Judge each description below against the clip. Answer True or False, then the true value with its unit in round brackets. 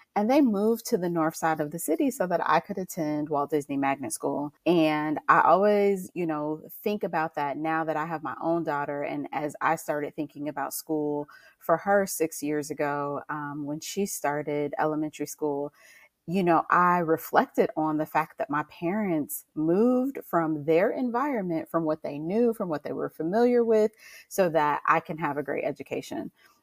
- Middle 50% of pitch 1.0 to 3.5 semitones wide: False (4.2 semitones)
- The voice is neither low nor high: True (160 Hz)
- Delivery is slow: False (190 wpm)